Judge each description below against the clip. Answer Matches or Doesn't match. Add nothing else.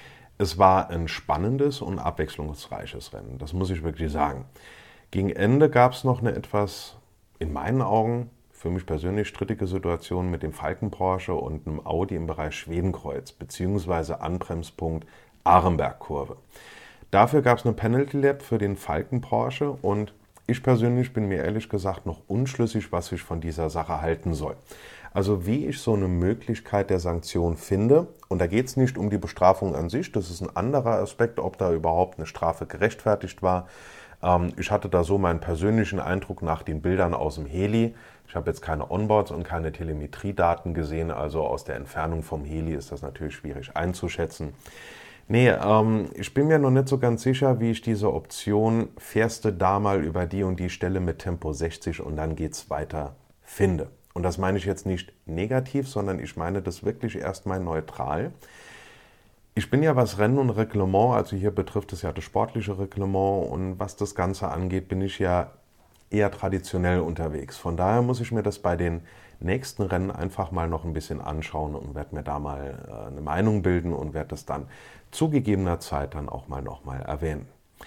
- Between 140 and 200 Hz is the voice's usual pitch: Doesn't match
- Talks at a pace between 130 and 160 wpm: Doesn't match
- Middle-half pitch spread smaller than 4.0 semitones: Doesn't match